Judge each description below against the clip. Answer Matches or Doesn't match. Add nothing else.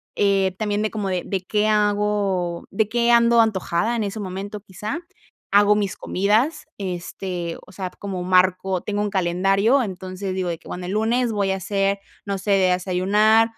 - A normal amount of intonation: Doesn't match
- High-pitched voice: Matches